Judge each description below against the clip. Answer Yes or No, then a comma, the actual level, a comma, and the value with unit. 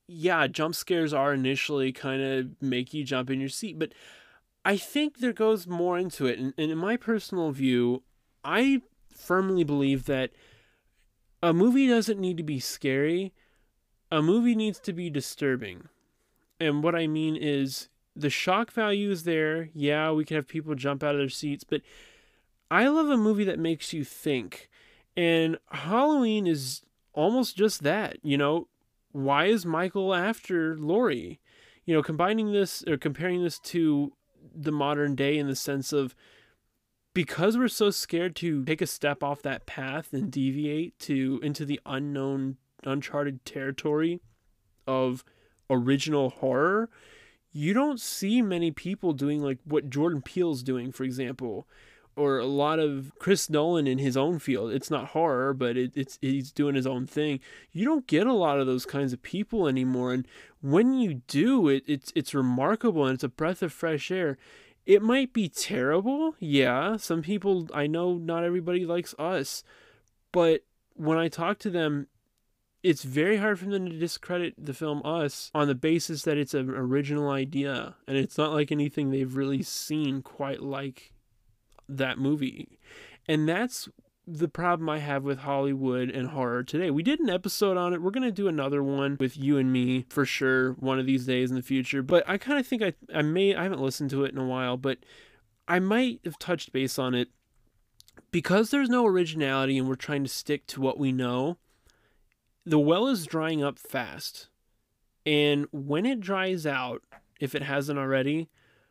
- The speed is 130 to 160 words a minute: No, average, 175 wpm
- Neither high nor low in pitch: Yes, medium, 150 Hz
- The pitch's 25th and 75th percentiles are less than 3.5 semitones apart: No, average, 4.7 semitones